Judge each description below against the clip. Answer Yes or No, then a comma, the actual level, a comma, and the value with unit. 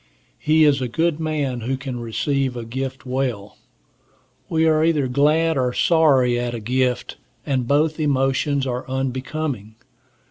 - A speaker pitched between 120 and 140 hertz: Yes, low, 135 Hz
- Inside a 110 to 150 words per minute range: Yes, average, 145 wpm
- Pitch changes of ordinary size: Yes, average, 3.4 semitones